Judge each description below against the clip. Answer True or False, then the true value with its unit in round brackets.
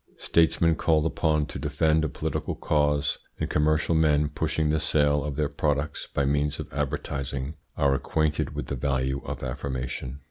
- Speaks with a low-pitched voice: True (75 Hz)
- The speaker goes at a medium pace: True (165 wpm)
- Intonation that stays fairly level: True (2.0 semitones)